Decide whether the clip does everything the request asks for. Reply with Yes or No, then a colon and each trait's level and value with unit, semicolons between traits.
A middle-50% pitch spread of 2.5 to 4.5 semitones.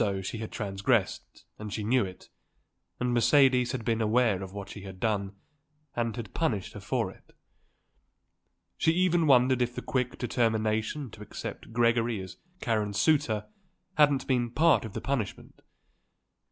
Yes: average, 3.4 semitones